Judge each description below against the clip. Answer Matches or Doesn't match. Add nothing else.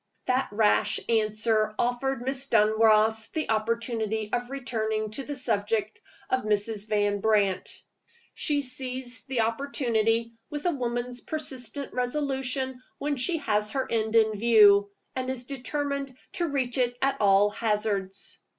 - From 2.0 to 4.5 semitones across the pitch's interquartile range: Matches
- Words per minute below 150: Matches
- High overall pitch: Matches